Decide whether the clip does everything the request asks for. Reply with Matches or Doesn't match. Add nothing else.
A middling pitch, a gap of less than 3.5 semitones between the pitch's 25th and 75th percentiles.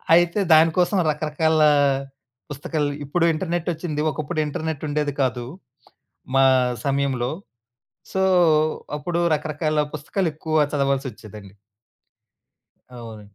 Matches